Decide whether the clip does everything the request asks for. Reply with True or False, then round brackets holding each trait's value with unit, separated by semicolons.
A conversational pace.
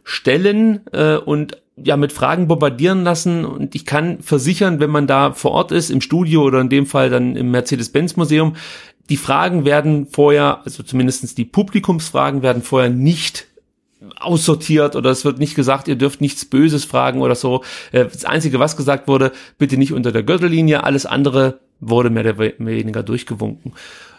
True (170 wpm)